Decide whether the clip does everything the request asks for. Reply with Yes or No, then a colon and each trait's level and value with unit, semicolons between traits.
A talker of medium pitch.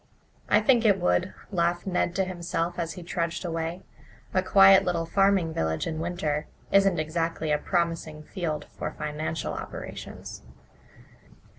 Yes: medium, 170 Hz